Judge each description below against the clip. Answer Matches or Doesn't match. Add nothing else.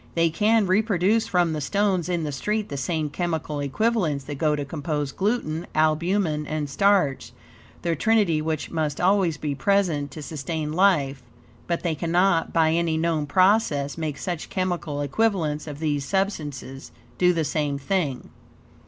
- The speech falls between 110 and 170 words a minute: Matches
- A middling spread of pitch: Matches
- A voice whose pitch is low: Doesn't match